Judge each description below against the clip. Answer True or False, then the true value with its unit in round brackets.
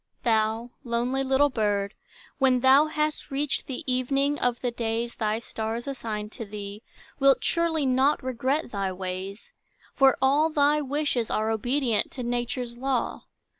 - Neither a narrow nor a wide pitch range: True (3.6 semitones)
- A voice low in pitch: False (250 Hz)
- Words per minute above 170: False (145 wpm)